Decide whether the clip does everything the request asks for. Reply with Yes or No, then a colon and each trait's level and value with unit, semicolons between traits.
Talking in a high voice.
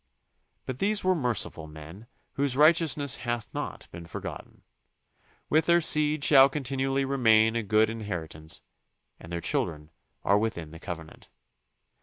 No: low, 115 Hz